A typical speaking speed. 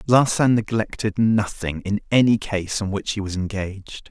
Yes: average, 160 wpm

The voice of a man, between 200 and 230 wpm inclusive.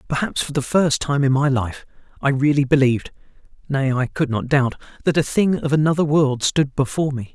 Yes: male; fast, 205 wpm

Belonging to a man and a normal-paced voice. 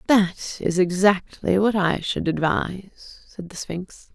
No: female; average, 145 wpm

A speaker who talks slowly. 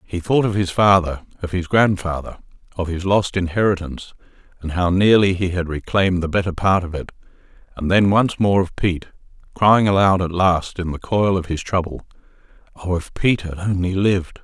No: average, 185 wpm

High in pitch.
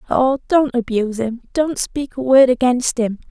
Yes: very high, 250 Hz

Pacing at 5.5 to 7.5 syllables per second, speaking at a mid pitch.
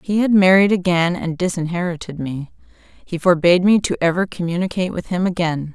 Yes: 5.8 syllables/s; medium, 175 Hz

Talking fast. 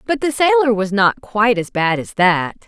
Yes: fast, 225 wpm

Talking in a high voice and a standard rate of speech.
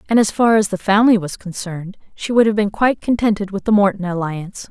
No: high, 200 Hz; fast, 230 wpm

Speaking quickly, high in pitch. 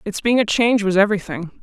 Yes: fast, 220 wpm; high, 205 Hz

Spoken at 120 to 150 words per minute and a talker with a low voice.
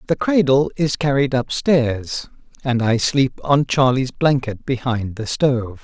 Yes: average, 145 wpm; low, 130 Hz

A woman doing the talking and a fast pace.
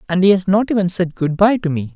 No: male; fast, 305 wpm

